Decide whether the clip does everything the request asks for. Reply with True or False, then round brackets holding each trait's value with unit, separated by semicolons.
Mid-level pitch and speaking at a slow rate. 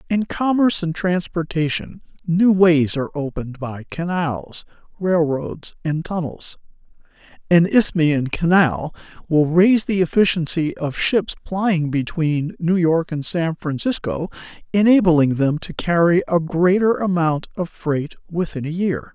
True (170 Hz; 130 wpm)